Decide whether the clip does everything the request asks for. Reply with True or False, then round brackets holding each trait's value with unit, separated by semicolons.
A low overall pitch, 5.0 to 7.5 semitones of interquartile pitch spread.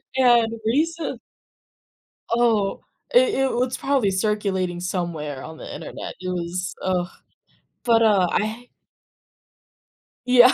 False (215 Hz; 5.3 semitones)